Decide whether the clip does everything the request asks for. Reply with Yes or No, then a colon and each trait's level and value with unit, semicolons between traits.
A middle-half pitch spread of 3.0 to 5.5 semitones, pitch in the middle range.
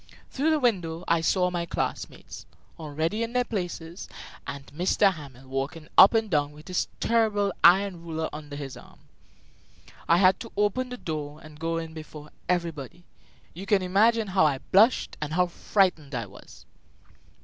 Yes: average, 4.7 semitones; medium, 170 Hz